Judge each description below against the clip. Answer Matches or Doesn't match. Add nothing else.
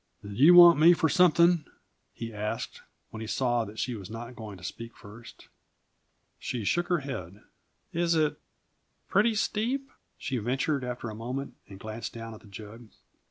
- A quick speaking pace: Doesn't match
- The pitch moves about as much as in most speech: Doesn't match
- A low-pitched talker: Matches